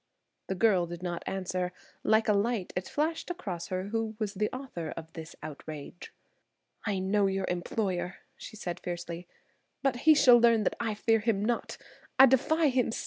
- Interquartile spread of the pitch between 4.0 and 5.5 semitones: Yes, average, 4.7 semitones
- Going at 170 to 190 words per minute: Yes, average, 180 wpm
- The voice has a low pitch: No, high, 205 Hz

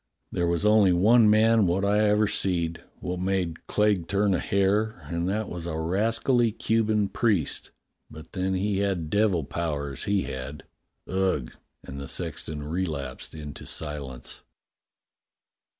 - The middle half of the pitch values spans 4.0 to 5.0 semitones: Yes, average, 4.6 semitones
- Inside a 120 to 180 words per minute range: Yes, average, 140 wpm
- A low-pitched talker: Yes, very low, 95 Hz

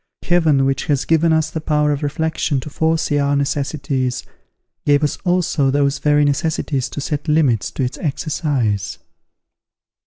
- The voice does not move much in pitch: Yes, narrow, 2.3 semitones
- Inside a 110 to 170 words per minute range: Yes, average, 150 wpm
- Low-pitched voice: No, medium, 145 Hz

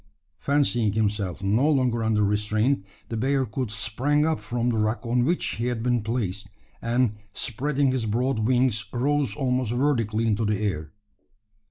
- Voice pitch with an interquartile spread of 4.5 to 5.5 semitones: No, average, 3.4 semitones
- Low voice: Yes, low, 120 Hz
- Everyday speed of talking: Yes, average, 155 wpm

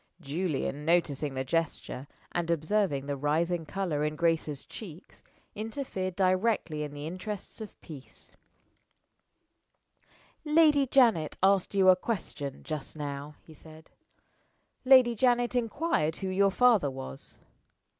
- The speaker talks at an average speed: No, slow, 120 wpm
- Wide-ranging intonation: Yes, wide, 5.9 semitones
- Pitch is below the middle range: No, medium, 170 Hz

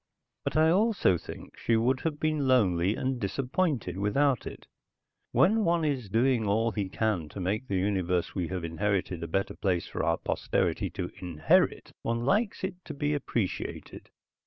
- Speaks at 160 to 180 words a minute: Yes, average, 170 wpm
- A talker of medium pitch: No, low, 115 Hz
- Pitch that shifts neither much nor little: No, wide, 7.5 semitones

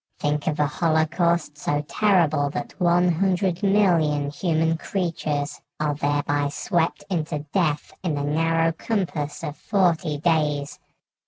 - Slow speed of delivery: Yes, slow, 130 wpm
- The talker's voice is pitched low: No, medium, 160 Hz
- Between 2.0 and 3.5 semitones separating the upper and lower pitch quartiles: Yes, average, 3.0 semitones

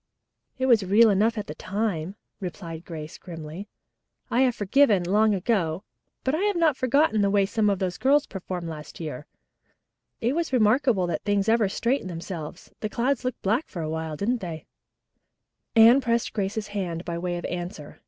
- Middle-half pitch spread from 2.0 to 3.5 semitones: No, average, 5.1 semitones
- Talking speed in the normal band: Yes, average, 175 wpm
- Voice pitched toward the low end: No, high, 200 Hz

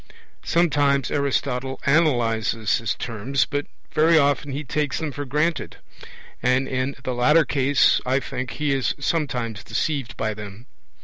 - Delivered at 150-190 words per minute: No, average, 140 wpm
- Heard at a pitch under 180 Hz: Yes, low, 135 Hz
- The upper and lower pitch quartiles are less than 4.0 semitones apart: Yes, average, 3.1 semitones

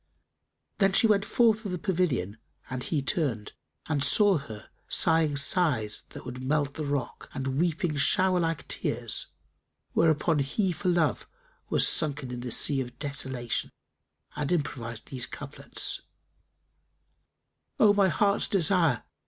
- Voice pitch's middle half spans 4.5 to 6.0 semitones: Yes, wide, 5.5 semitones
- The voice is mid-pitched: Yes, medium, 150 Hz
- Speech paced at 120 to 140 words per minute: Yes, slow, 135 wpm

